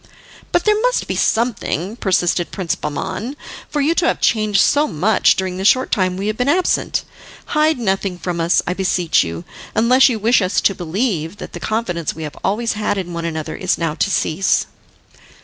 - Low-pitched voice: No, high, 195 Hz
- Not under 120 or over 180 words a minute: No, average, 195 wpm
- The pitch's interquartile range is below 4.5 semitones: No, average, 5.3 semitones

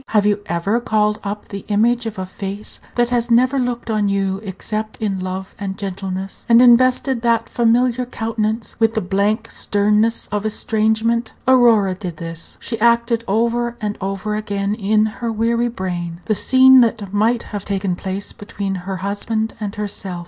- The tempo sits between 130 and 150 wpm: No, average, 170 wpm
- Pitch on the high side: Yes, high, 215 Hz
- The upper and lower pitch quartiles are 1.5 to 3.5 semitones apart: Yes, average, 2.8 semitones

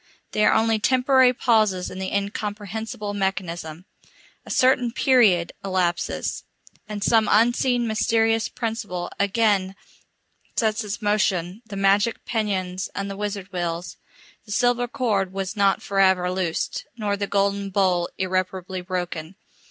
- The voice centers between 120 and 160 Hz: No, high, 200 Hz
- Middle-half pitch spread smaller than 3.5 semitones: Yes, average, 3.0 semitones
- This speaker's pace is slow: Yes, slow, 130 wpm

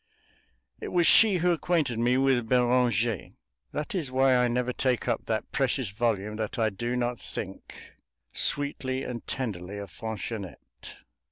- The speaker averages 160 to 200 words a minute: No, average, 150 wpm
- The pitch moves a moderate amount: Yes, average, 3.0 semitones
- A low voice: Yes, low, 125 Hz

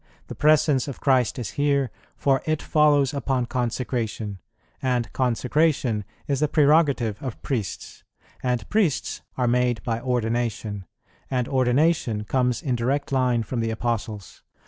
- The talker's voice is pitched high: No, low, 125 Hz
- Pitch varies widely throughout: No, average, 3.3 semitones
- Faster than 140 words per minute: No, slow, 135 wpm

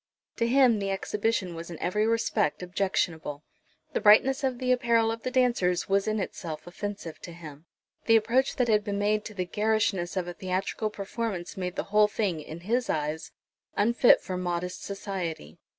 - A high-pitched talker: Yes, high, 200 Hz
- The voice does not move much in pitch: No, average, 4.3 semitones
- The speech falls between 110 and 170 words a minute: No, average, 180 wpm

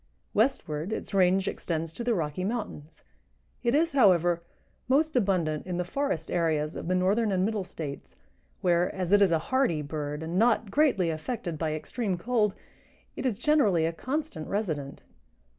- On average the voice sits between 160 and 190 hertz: Yes, medium, 185 Hz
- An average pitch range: No, wide, 6.1 semitones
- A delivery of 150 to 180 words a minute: Yes, average, 165 wpm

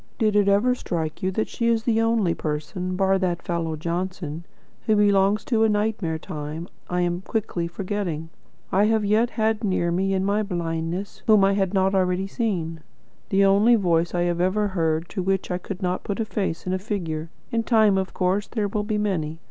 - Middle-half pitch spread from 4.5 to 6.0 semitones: No, average, 3.3 semitones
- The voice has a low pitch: No, high, 190 Hz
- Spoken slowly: No, average, 200 wpm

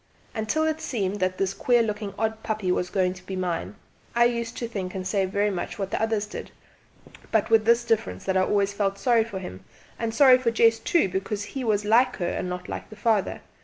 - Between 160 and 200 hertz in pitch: No, high, 210 Hz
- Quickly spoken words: Yes, fast, 230 wpm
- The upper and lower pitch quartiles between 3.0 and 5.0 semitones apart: Yes, average, 3.3 semitones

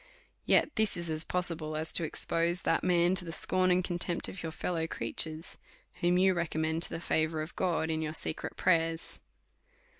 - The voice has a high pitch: No, medium, 170 Hz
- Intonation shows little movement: Yes, narrow, 2.0 semitones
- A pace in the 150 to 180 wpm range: No, average, 190 wpm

